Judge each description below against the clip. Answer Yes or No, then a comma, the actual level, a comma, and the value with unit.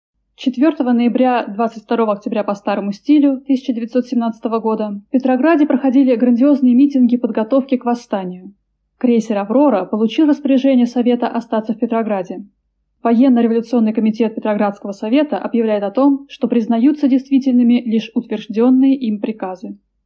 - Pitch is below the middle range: No, high, 240 Hz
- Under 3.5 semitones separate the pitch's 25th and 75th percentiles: Yes, average, 3.1 semitones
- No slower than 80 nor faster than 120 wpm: Yes, average, 115 wpm